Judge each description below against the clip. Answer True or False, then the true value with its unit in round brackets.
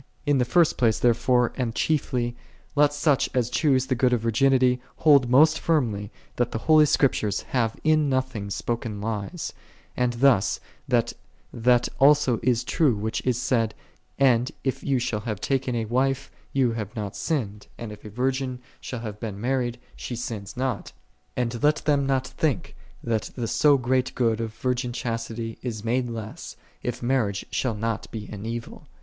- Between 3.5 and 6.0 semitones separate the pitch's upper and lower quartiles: False (2.8 semitones)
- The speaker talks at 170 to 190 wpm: True (180 wpm)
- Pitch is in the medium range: False (125 Hz)